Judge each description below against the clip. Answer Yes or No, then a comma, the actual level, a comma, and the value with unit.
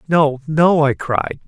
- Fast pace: No, average, 165 wpm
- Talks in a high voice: No, medium, 150 Hz